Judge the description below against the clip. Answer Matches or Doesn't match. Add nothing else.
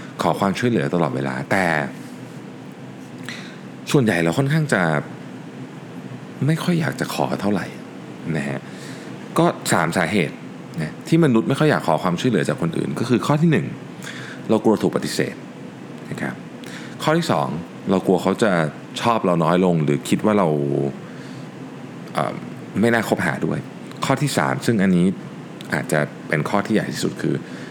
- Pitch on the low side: Matches